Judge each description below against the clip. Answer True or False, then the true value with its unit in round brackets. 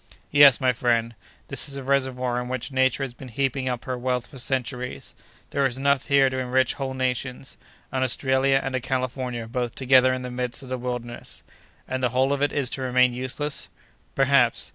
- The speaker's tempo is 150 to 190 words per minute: False (200 wpm)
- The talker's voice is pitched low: True (130 Hz)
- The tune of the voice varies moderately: False (1.2 semitones)